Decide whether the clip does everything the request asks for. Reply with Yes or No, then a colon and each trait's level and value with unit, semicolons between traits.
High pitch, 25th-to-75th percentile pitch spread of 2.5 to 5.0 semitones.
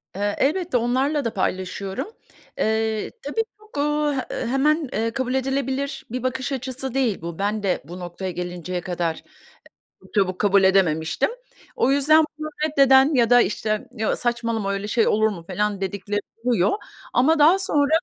No: high, 235 Hz; wide, 5.6 semitones